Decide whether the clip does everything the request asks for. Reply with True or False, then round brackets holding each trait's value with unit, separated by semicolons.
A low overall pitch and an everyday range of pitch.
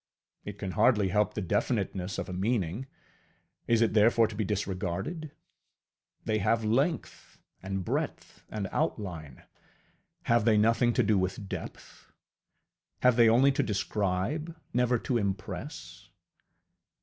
True (105 Hz; 3.6 semitones)